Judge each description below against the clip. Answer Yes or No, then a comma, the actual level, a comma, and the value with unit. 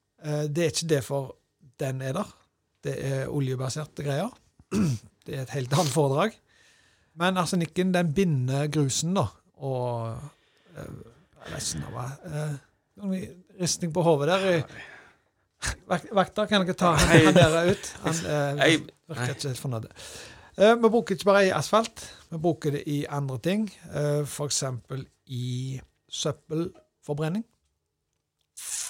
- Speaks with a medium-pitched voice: Yes, medium, 150 Hz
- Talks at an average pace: No, slow, 125 wpm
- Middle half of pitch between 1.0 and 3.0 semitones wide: No, average, 4.6 semitones